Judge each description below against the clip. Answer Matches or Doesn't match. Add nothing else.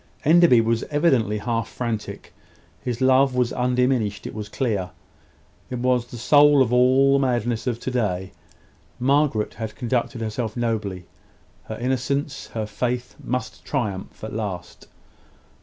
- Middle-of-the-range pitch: Doesn't match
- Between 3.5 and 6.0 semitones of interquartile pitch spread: Doesn't match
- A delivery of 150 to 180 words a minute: Doesn't match